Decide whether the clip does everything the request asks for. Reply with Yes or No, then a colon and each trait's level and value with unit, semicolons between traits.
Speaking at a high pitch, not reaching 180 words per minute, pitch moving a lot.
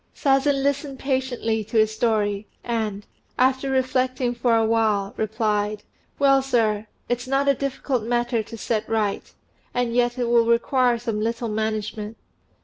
No: high, 235 Hz; average, 145 wpm; average, 3.0 semitones